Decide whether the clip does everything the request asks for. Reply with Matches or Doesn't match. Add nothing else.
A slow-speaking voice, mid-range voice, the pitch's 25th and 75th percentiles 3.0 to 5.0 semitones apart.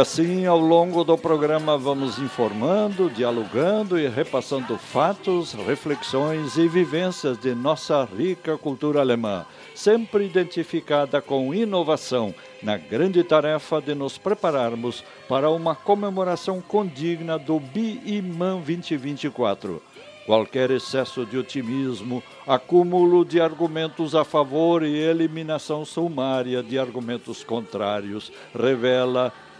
Matches